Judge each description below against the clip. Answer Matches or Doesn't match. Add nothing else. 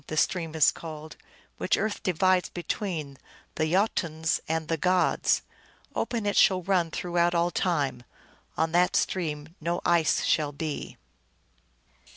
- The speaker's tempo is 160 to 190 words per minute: Doesn't match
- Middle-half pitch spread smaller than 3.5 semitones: Matches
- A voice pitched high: Doesn't match